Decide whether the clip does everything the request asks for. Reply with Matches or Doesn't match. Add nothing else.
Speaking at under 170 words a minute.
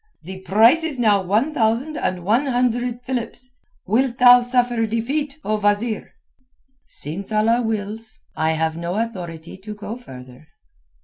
Matches